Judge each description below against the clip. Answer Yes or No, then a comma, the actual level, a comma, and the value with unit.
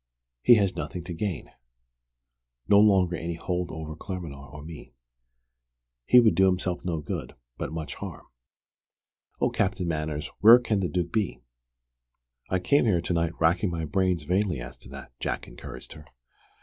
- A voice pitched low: Yes, very low, 85 Hz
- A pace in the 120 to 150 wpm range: No, average, 160 wpm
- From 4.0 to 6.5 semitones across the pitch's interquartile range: No, average, 3.4 semitones